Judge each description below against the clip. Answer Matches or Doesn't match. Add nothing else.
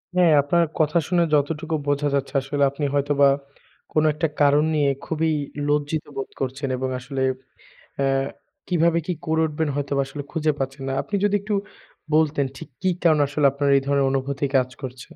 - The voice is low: Doesn't match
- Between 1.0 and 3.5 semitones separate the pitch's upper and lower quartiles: Matches